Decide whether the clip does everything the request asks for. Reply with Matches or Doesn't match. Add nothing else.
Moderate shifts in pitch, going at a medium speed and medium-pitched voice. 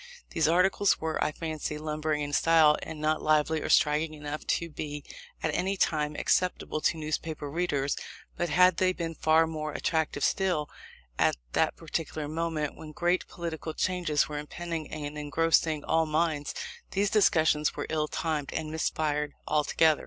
Doesn't match